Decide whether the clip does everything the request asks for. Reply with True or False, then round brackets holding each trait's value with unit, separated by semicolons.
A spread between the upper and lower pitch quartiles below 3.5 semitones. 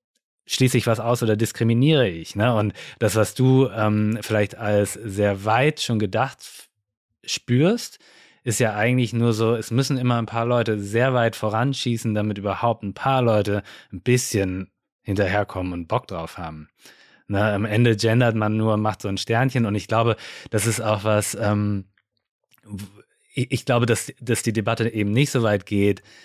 True (2.7 semitones)